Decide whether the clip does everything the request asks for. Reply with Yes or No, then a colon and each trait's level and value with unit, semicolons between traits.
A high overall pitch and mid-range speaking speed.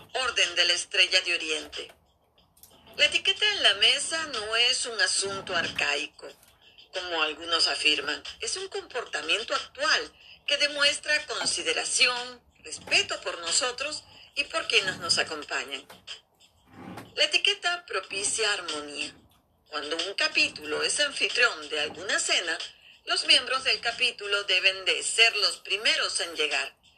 No: very high, 250 Hz; slow, 125 wpm